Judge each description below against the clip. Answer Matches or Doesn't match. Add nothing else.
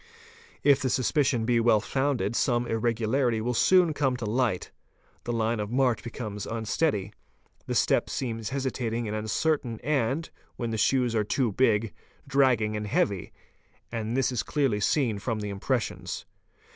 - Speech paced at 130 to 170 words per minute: Matches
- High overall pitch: Doesn't match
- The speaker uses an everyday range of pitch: Matches